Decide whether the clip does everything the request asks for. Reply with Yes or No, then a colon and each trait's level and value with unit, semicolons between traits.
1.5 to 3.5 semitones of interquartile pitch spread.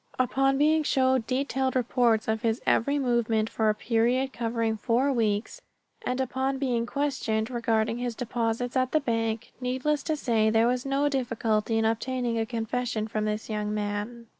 Yes: average, 2.7 semitones